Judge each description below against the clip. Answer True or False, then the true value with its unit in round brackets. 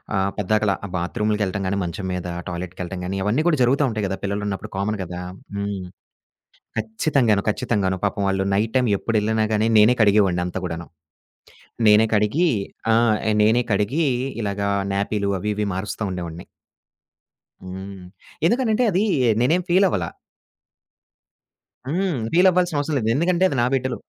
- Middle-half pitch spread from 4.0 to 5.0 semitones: True (4.6 semitones)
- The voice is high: False (105 Hz)